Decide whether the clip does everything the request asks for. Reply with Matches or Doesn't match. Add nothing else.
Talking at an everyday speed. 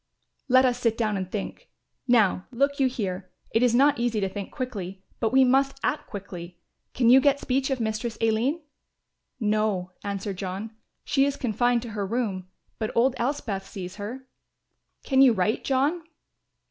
Matches